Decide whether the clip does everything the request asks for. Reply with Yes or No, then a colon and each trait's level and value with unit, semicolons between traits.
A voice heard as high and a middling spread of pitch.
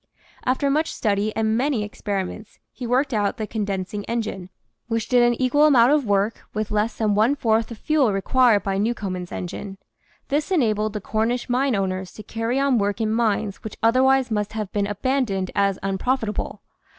Yes: high, 220 Hz; average, 3.6 semitones